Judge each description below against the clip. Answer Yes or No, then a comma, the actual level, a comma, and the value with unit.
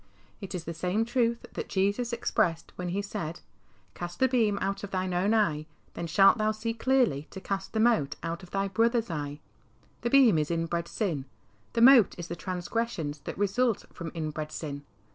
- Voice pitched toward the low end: No, high, 190 Hz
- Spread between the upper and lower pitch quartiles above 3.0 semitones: Yes, average, 5.3 semitones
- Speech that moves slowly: No, average, 195 wpm